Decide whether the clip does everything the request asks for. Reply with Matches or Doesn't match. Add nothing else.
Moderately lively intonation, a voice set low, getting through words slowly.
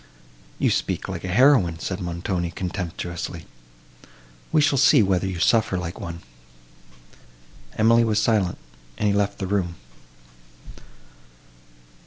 Matches